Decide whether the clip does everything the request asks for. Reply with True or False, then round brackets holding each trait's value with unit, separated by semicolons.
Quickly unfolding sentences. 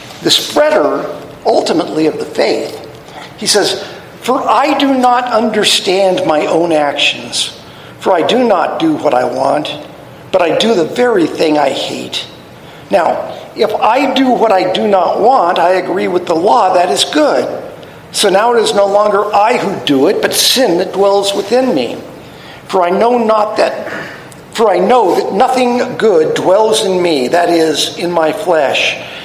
False (170 wpm)